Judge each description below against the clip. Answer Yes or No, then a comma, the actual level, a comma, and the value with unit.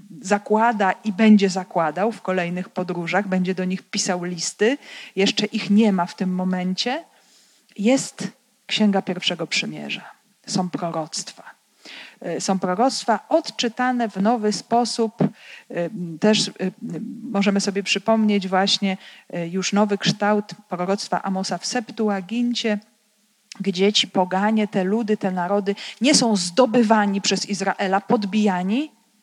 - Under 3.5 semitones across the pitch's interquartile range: Yes, average, 2.8 semitones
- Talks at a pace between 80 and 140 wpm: Yes, average, 115 wpm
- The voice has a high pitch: Yes, high, 205 Hz